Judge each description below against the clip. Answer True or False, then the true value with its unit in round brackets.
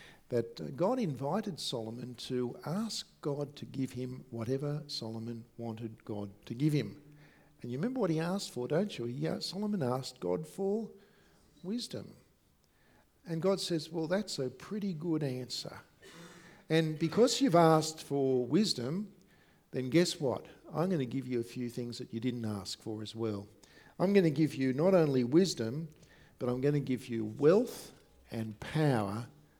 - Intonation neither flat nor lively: False (6.4 semitones)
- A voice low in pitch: False (145 Hz)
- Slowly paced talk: False (165 wpm)